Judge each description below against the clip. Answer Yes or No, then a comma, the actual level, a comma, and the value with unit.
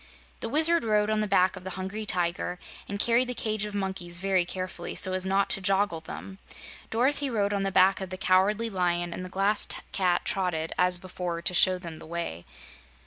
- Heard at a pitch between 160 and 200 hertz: Yes, high, 190 Hz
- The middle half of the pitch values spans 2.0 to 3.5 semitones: Yes, narrow, 2.5 semitones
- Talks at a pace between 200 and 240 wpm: Yes, fast, 205 wpm